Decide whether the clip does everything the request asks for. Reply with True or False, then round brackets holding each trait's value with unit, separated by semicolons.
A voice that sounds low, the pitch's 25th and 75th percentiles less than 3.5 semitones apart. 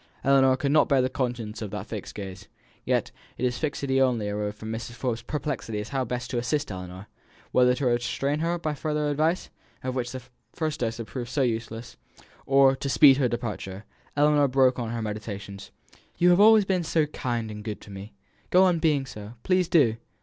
False (125 Hz; 4.7 semitones)